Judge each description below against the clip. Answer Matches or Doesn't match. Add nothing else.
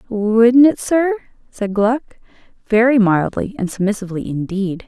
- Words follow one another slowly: Matches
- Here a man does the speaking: Doesn't match